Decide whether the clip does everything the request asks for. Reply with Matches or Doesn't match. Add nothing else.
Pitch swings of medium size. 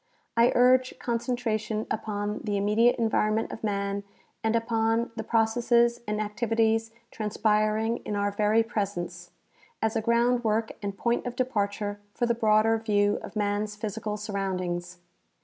Doesn't match